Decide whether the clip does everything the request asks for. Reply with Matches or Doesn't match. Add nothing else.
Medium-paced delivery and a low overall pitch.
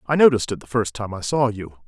Doesn't match